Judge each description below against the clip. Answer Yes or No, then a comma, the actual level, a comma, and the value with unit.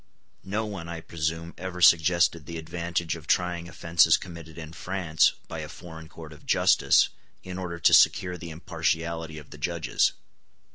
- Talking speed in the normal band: Yes, average, 160 wpm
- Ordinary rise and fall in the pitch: No, narrow, 1.4 semitones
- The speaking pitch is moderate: No, very low, 85 Hz